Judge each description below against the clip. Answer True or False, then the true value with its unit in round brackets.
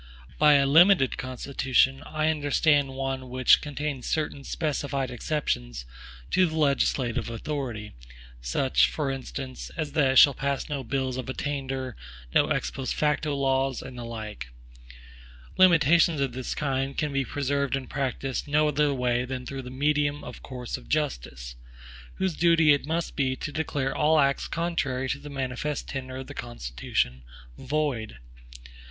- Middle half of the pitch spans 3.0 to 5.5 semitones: False (2.5 semitones)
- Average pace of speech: True (155 wpm)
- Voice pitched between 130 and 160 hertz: True (135 Hz)